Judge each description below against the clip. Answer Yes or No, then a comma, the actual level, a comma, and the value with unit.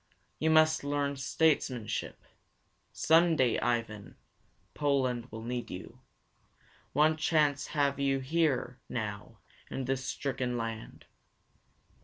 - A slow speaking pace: Yes, slow, 105 wpm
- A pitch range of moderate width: Yes, average, 3.7 semitones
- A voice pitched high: No, low, 135 Hz